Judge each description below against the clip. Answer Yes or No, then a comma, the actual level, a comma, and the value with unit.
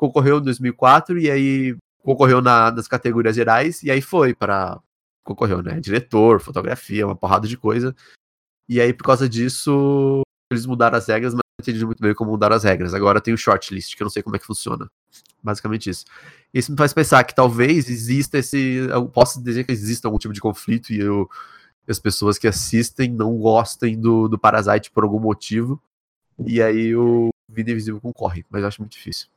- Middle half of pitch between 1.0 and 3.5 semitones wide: Yes, average, 2.9 semitones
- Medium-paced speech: No, fast, 200 wpm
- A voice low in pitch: Yes, low, 115 Hz